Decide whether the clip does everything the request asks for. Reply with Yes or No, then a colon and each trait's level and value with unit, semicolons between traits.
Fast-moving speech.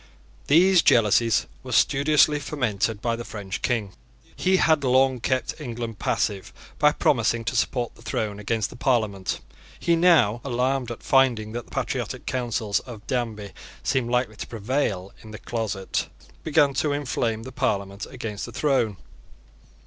No: average, 150 wpm